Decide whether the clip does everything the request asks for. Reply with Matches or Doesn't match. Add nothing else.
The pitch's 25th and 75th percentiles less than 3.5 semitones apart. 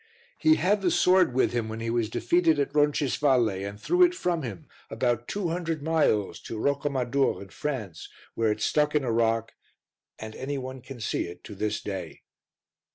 Doesn't match